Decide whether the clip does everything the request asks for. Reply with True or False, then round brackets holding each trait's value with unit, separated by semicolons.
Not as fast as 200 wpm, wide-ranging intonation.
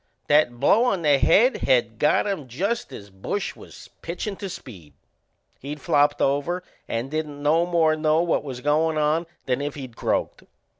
False (170 wpm; 4.1 semitones)